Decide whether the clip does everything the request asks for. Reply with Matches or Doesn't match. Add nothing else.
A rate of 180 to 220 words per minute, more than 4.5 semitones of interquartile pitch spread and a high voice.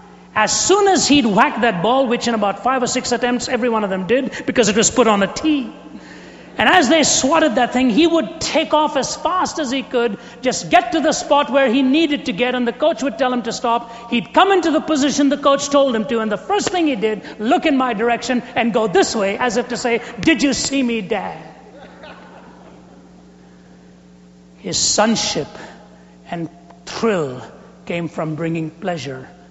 Matches